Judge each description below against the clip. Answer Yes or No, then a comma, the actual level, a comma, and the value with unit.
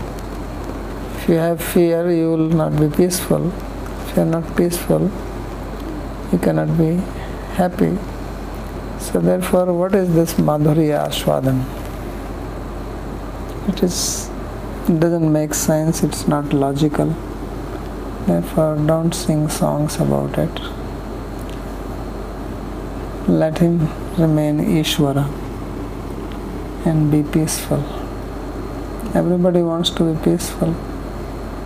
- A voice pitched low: No, medium, 155 Hz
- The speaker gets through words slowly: Yes, slow, 95 wpm